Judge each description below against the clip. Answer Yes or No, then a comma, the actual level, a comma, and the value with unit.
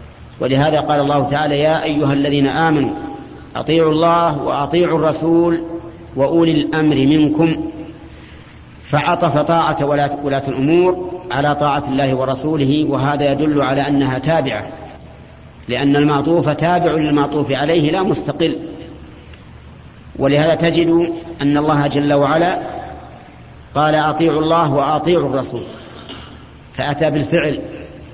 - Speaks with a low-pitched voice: No, medium, 150 Hz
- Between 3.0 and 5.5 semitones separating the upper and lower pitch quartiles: No, narrow, 2.4 semitones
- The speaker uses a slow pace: No, average, 100 wpm